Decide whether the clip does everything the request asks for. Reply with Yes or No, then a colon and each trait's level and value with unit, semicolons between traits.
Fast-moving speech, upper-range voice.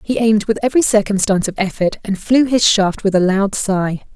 Yes: fast, 215 wpm; high, 205 Hz